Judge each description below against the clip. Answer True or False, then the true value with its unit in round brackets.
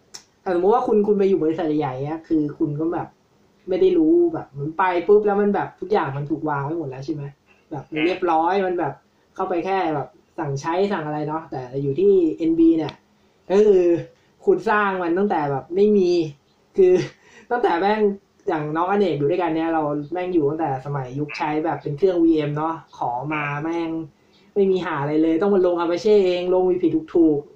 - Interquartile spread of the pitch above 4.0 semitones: True (4.6 semitones)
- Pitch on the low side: False (170 Hz)